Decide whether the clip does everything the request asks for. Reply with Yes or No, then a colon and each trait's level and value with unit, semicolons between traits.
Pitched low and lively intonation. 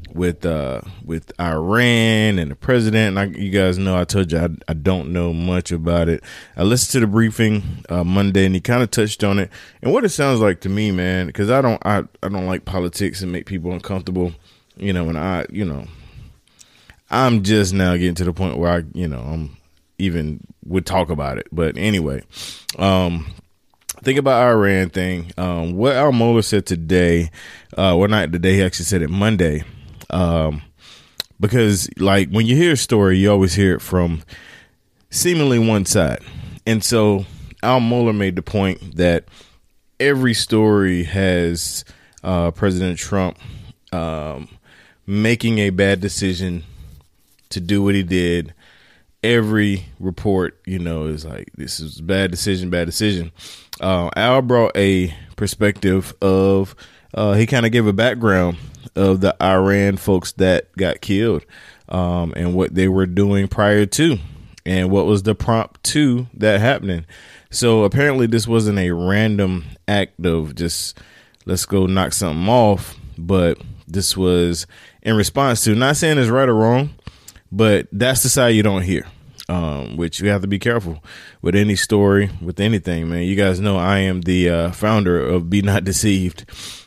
No: very low, 95 Hz; average, 3.3 semitones